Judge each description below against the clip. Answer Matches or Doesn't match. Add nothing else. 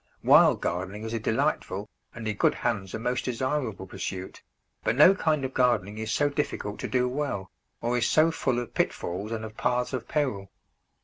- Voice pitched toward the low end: Matches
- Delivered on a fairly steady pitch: Doesn't match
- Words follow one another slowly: Doesn't match